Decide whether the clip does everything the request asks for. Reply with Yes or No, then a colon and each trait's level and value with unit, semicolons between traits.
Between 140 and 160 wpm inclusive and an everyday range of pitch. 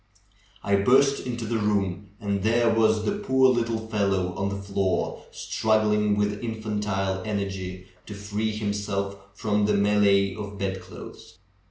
No: average, 145 wpm; narrow, 1.9 semitones